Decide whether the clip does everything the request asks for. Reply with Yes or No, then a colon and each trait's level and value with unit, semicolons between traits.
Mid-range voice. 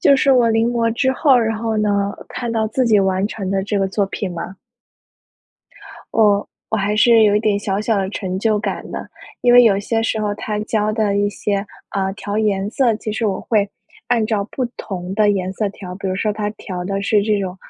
No: high, 210 Hz